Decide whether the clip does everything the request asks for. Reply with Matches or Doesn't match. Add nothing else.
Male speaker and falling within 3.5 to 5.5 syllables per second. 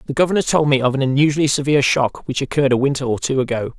Doesn't match